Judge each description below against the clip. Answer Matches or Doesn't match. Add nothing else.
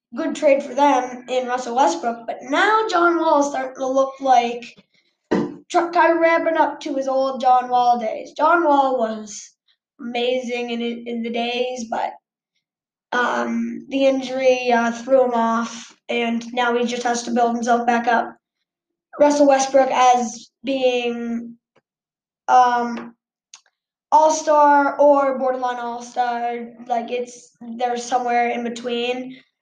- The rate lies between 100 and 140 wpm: Matches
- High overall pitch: Matches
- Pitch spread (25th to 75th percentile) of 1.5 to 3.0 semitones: Matches